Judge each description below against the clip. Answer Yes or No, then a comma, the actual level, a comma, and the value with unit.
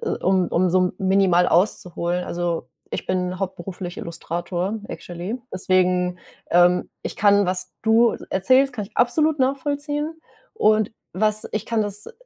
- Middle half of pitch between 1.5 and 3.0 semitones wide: No, average, 3.7 semitones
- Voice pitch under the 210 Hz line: Yes, high, 190 Hz